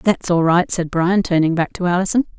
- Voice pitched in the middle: Yes, medium, 180 Hz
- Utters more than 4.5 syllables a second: Yes, 5.3 syllables/s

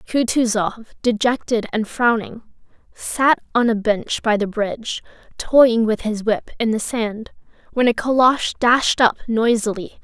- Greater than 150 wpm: No, average, 145 wpm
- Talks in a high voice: Yes, high, 230 Hz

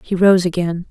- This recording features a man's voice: No, female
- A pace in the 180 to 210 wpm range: Yes, average, 200 wpm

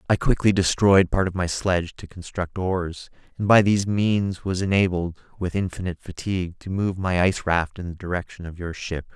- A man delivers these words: Yes, male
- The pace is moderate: Yes, average, 195 wpm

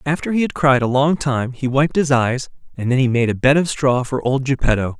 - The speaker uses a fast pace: Yes, fast, 265 wpm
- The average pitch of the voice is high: No, low, 135 Hz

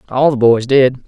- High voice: No, low, 130 Hz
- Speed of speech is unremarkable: No, fast, 225 wpm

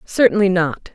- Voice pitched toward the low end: No, high, 190 Hz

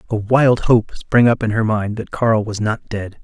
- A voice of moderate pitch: No, low, 110 Hz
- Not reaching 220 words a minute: No, fast, 240 wpm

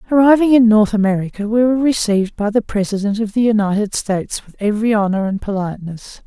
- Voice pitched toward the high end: Yes, high, 215 Hz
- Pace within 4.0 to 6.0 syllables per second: No, 6.3 syllables/s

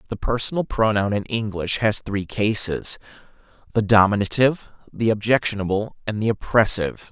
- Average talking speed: No, slow, 125 wpm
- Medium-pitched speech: No, low, 105 Hz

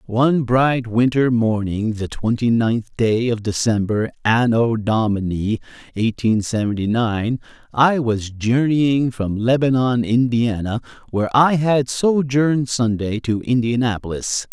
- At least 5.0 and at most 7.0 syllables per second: No, 4.0 syllables/s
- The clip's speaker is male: Yes, male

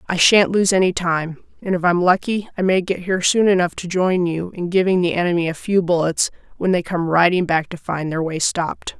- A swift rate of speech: Yes, fast, 235 wpm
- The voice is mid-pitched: Yes, medium, 180 Hz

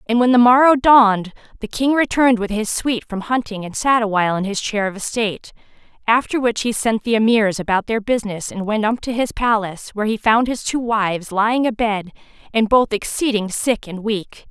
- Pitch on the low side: No, high, 220 Hz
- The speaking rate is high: Yes, fast, 210 wpm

